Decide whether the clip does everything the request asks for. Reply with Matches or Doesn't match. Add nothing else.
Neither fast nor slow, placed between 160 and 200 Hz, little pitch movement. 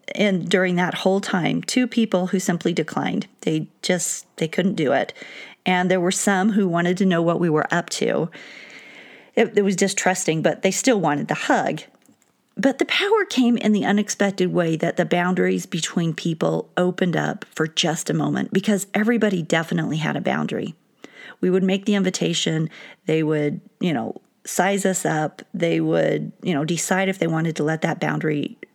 Doesn't match